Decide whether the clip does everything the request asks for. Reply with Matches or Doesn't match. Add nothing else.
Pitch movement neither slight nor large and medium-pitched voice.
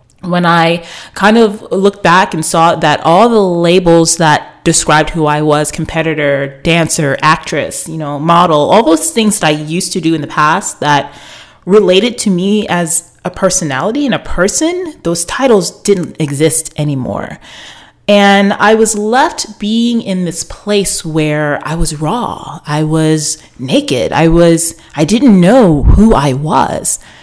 Matches